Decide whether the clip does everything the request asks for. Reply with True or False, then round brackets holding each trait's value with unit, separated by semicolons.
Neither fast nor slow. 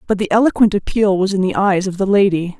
False (255 wpm)